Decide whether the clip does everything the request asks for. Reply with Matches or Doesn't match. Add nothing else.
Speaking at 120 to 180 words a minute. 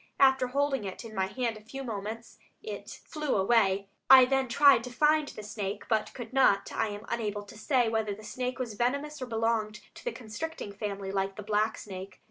Doesn't match